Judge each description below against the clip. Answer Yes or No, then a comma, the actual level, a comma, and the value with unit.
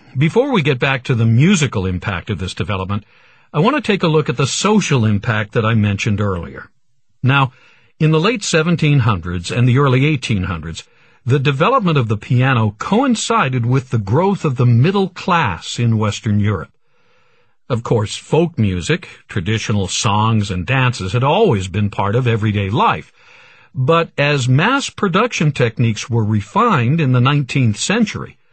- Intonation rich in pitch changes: Yes, wide, 6.5 semitones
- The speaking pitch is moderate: No, low, 125 Hz